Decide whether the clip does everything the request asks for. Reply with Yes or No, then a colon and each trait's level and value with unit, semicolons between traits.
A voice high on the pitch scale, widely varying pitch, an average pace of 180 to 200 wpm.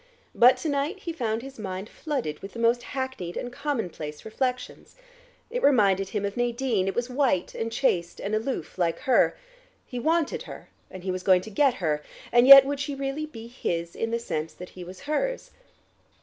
Yes: high, 235 Hz; wide, 6.4 semitones; average, 195 wpm